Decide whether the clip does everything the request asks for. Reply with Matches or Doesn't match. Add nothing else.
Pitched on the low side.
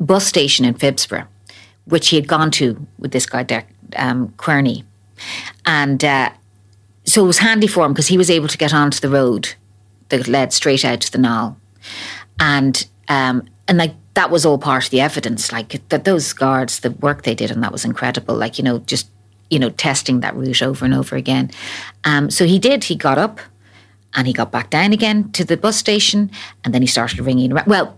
Matches